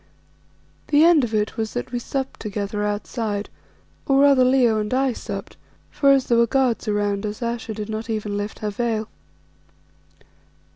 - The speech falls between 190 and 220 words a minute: No, average, 165 wpm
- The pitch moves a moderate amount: Yes, average, 3.4 semitones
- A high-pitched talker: Yes, high, 225 Hz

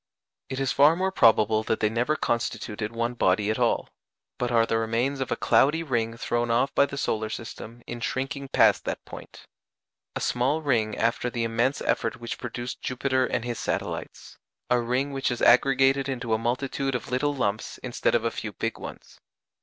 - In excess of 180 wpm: Yes, average, 190 wpm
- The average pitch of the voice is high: No, low, 120 Hz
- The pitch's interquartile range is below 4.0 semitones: Yes, average, 2.8 semitones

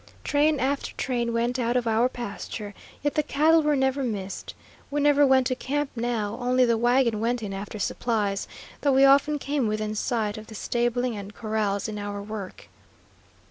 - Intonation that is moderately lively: Yes, average, 4.0 semitones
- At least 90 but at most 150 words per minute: No, average, 180 wpm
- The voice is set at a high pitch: Yes, high, 240 Hz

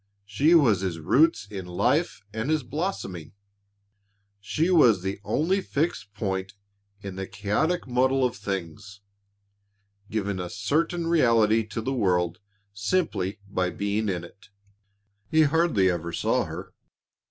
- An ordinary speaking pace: No, slow, 130 wpm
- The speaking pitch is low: Yes, low, 105 Hz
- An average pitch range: No, wide, 7.5 semitones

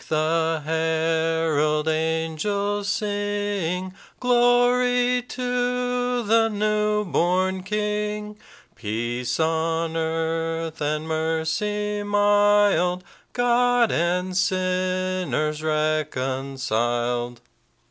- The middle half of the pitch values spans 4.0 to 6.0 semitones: Yes, average, 4.7 semitones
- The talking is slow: Yes, slow, 65 wpm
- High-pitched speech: No, medium, 180 Hz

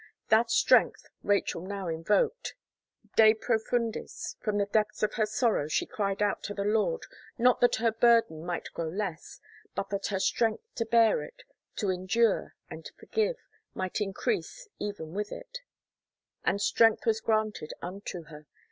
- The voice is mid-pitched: No, high, 215 Hz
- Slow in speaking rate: No, average, 155 wpm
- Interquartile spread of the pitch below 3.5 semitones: Yes, average, 3.1 semitones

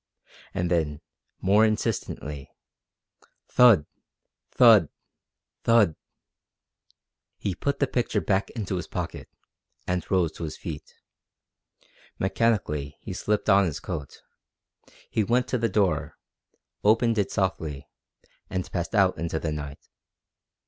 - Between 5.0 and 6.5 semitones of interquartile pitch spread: Yes, wide, 5.5 semitones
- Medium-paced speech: No, slow, 115 wpm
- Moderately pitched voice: No, very low, 95 Hz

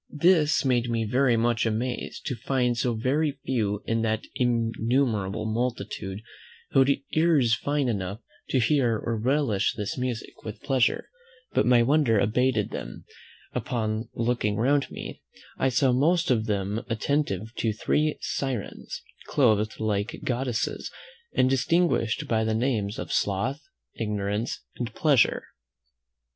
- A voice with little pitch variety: No, average, 3.5 semitones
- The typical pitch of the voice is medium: No, low, 120 Hz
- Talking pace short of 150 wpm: Yes, slow, 135 wpm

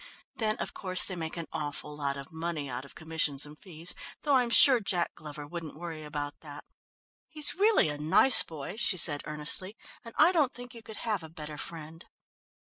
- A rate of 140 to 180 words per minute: No, average, 200 wpm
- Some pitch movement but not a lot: No, wide, 6.2 semitones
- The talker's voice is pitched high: No, medium, 160 Hz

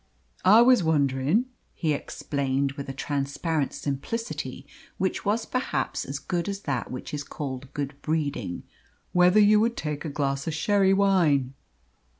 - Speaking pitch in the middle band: Yes, medium, 150 Hz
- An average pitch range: No, wide, 5.9 semitones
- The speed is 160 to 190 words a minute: No, average, 150 wpm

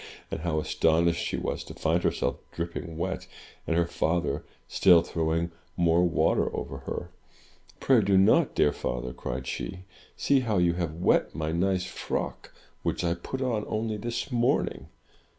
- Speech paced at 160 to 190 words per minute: Yes, average, 170 wpm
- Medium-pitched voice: No, very low, 85 Hz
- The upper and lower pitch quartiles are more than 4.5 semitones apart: No, average, 3.0 semitones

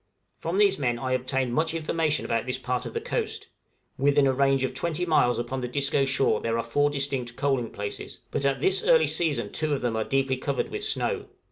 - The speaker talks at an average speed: No, fast, 220 wpm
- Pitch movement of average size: Yes, average, 3.2 semitones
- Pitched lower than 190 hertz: Yes, low, 135 Hz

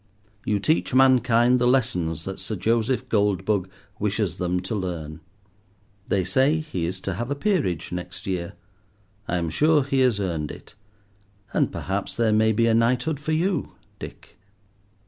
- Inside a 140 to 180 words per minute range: Yes, average, 160 wpm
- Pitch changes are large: Yes, wide, 6.0 semitones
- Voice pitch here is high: No, low, 110 Hz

